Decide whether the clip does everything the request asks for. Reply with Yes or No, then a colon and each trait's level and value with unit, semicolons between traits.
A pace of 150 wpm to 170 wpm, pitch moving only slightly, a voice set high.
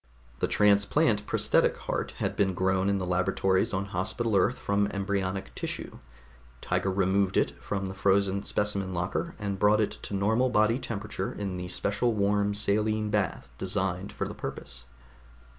No: average, 160 wpm; narrow, 1.6 semitones; low, 100 Hz